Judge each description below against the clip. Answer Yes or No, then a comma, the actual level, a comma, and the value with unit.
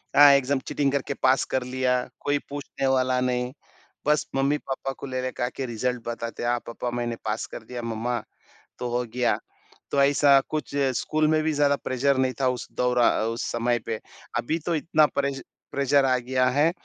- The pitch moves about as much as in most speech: No, narrow, 2.3 semitones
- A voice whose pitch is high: No, low, 130 Hz